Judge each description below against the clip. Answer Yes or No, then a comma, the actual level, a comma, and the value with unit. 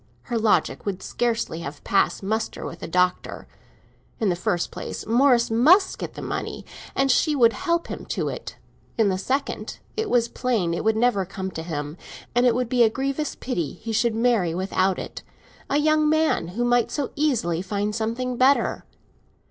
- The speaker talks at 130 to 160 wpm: No, average, 180 wpm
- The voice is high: Yes, high, 230 Hz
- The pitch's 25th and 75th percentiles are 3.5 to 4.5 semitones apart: No, average, 5.2 semitones